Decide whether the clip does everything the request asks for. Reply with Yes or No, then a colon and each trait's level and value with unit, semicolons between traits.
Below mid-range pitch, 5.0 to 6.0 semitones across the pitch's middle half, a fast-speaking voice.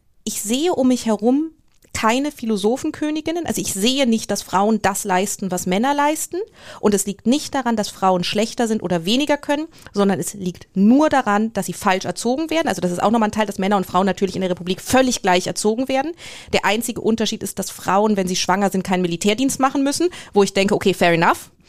No: high, 210 Hz; wide, 5.5 semitones; fast, 220 wpm